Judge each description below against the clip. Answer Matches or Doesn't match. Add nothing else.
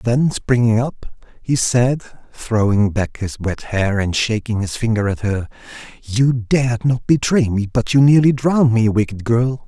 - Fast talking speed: Doesn't match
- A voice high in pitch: Doesn't match